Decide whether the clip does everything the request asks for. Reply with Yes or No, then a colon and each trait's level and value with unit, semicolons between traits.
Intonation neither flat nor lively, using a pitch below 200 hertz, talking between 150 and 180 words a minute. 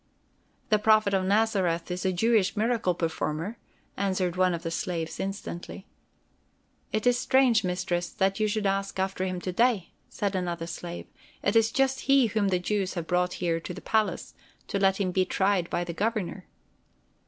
Yes: average, 3.3 semitones; high, 190 Hz; average, 175 wpm